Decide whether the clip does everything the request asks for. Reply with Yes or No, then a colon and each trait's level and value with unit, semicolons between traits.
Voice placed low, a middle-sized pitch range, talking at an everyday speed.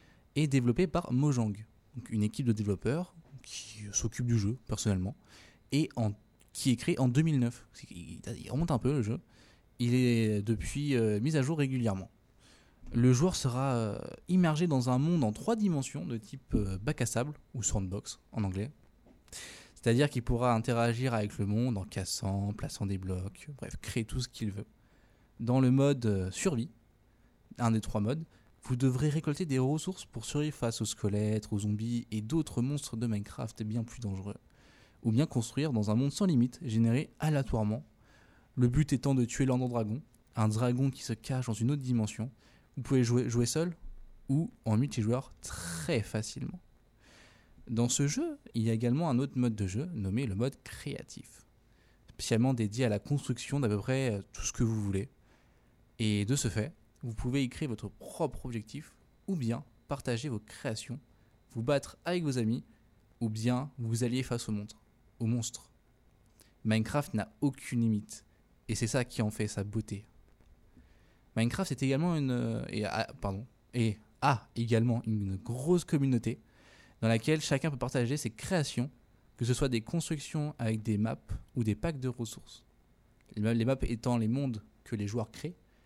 Yes: low, 120 Hz; average, 3.7 semitones; average, 175 wpm